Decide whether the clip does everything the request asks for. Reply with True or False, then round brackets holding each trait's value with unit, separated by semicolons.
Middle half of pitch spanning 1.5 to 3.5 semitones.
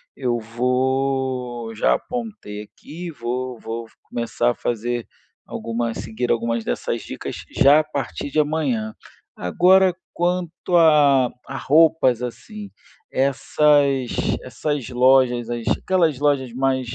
False (4.1 semitones)